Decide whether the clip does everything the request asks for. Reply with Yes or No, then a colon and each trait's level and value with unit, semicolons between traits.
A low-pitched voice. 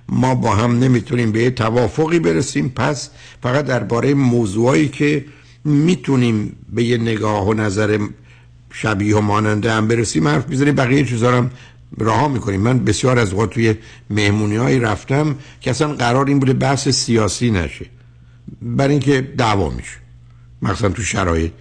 Yes: low, 120 Hz